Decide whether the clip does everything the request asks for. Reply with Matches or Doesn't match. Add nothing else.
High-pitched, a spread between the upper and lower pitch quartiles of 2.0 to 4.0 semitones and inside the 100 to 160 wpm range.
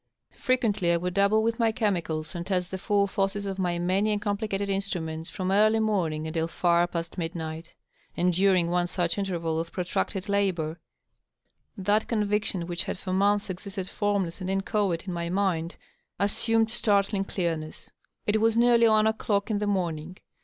Doesn't match